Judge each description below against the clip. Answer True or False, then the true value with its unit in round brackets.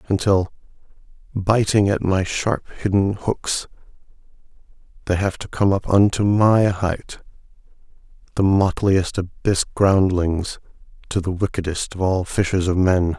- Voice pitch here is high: False (95 Hz)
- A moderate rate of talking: False (125 wpm)